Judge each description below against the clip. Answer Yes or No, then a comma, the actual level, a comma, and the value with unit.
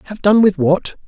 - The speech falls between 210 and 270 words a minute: Yes, fast, 220 wpm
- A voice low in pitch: No, high, 190 Hz